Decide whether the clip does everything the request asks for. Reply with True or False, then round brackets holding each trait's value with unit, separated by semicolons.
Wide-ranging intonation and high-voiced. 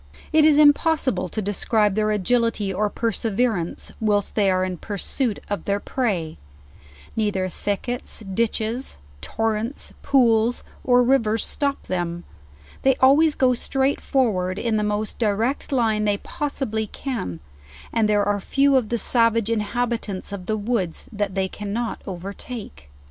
False (3.5 semitones; 220 Hz)